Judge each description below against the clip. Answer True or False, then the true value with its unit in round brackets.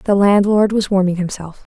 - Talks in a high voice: True (195 Hz)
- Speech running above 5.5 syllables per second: False (5.0 syllables/s)